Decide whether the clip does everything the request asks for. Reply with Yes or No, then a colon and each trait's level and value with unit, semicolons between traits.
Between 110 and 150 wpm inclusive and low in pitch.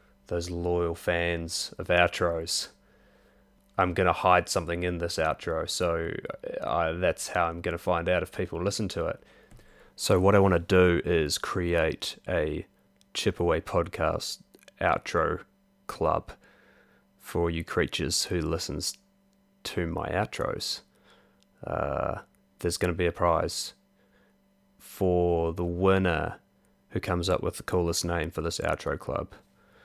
Yes: slow, 135 wpm; very low, 90 Hz